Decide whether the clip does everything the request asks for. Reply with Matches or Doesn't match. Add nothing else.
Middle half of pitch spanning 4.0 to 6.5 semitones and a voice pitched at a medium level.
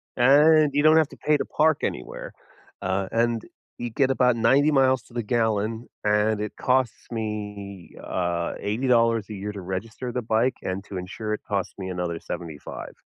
Doesn't match